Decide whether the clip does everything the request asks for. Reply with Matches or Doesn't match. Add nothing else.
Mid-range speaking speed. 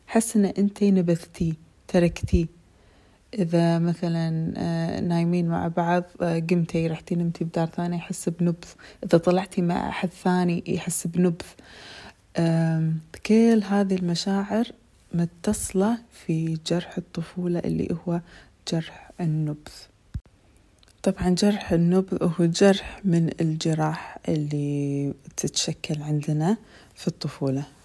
Matches